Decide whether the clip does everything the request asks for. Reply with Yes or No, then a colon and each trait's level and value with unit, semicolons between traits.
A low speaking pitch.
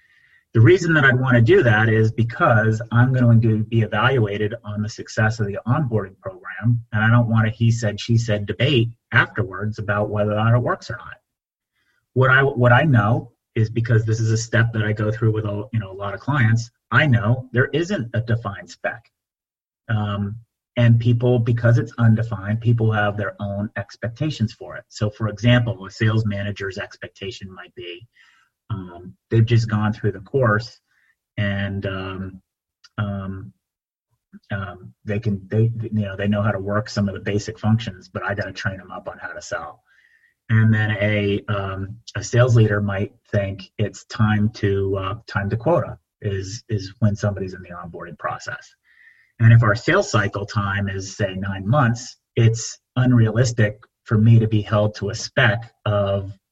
Yes: low, 110 Hz